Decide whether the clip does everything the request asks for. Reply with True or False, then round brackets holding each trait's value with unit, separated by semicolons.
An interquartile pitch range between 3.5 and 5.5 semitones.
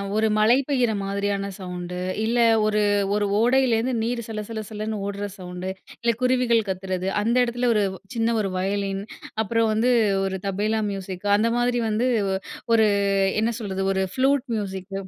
False (3.1 semitones)